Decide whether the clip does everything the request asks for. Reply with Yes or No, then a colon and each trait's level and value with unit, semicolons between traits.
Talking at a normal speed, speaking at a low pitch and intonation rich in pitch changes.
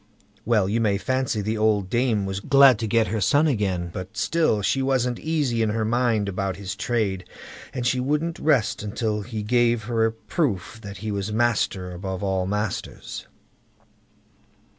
No: average, 170 wpm; low, 110 Hz; average, 3.6 semitones